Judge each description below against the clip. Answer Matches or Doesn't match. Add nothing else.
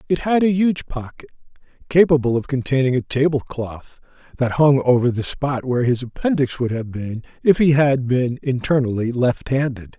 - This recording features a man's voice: Matches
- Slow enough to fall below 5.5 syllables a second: Matches